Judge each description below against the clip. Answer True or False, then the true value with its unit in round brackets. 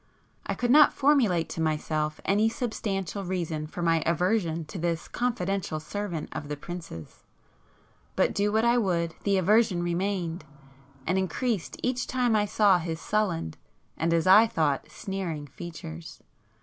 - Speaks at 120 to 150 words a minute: True (145 wpm)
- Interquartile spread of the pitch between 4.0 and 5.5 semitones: True (4.3 semitones)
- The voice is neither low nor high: True (180 Hz)